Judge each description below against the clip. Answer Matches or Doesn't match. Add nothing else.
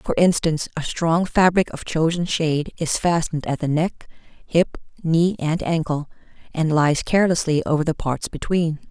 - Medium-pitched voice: Matches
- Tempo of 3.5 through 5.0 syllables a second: Matches